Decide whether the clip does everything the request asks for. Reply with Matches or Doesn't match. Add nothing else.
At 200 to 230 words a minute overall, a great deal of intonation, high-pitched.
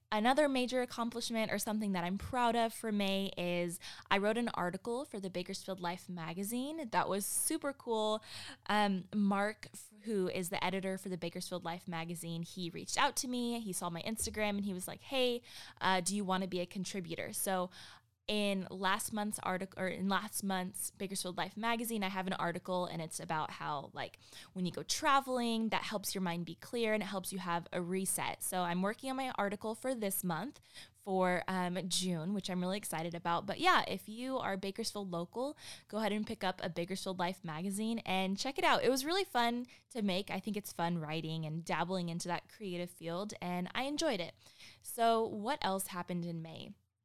Doesn't match